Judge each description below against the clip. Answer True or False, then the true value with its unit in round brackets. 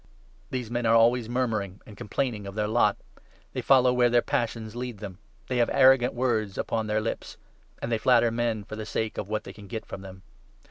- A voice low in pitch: True (115 Hz)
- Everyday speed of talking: False (225 wpm)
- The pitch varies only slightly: True (2.3 semitones)